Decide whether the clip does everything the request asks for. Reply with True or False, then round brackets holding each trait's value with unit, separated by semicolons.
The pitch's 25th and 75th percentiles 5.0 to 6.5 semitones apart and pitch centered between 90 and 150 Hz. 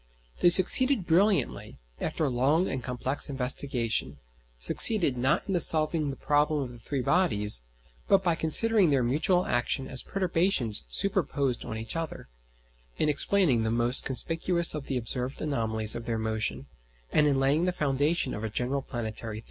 True (5.6 semitones; 140 Hz)